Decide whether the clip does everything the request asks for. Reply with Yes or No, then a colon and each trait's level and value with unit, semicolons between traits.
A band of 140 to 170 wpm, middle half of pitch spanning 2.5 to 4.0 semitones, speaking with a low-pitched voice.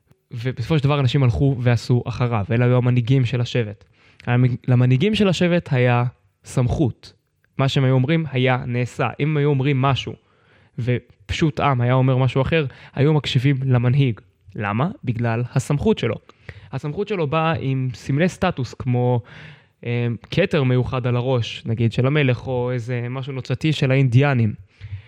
Yes: average, 145 wpm; average, 2.8 semitones; low, 130 Hz